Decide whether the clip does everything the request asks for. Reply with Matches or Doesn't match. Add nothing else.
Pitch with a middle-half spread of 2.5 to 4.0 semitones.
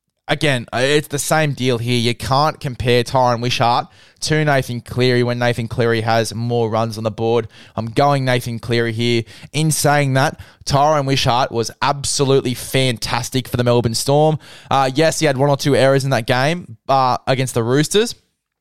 Matches